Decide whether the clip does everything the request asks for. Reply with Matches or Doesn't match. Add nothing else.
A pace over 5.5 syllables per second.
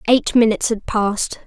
Doesn't match